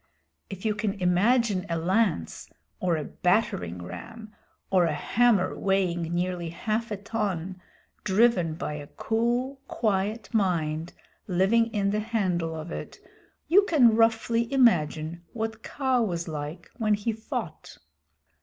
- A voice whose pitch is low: No, high, 200 Hz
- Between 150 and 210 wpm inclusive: No, slow, 135 wpm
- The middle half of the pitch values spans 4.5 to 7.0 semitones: Yes, average, 4.8 semitones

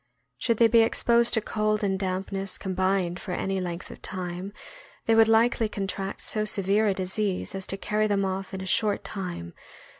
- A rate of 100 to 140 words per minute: No, average, 185 wpm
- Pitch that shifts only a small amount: Yes, narrow, 2.3 semitones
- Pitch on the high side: Yes, high, 195 Hz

